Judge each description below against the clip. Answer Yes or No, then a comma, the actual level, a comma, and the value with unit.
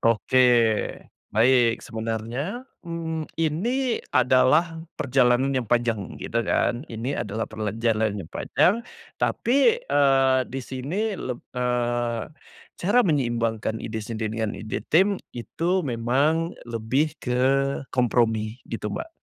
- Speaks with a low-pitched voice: Yes, low, 125 Hz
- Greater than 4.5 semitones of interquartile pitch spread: Yes, wide, 5.6 semitones